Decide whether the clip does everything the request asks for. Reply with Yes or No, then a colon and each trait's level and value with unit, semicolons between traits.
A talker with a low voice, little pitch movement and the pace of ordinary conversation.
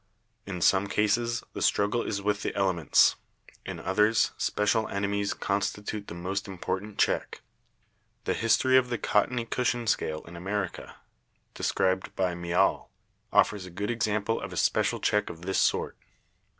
Yes: low, 100 Hz; narrow, 2.3 semitones; average, 150 wpm